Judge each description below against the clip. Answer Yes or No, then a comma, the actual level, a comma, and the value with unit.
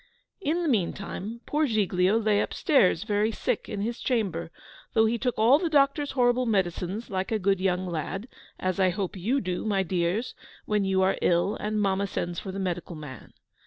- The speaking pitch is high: Yes, high, 200 Hz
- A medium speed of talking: Yes, average, 190 wpm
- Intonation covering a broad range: No, average, 3.8 semitones